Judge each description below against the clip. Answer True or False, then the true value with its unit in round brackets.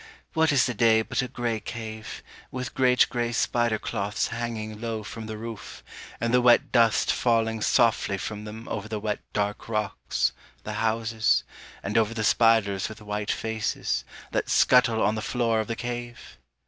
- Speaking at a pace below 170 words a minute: False (175 wpm)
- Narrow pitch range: True (1.7 semitones)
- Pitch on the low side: True (110 Hz)